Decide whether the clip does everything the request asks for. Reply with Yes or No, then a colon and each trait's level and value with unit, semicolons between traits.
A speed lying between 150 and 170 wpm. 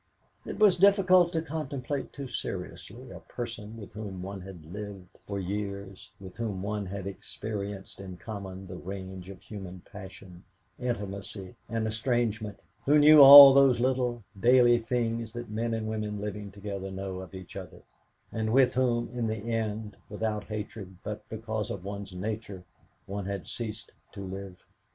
Yes: average, 160 wpm